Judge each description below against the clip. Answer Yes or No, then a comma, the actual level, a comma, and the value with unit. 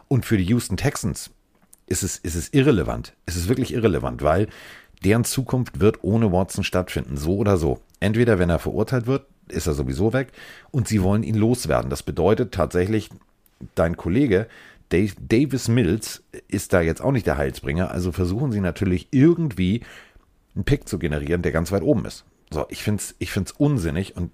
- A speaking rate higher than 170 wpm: Yes, average, 185 wpm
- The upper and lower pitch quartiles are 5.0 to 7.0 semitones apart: Yes, wide, 5.4 semitones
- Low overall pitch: Yes, low, 100 Hz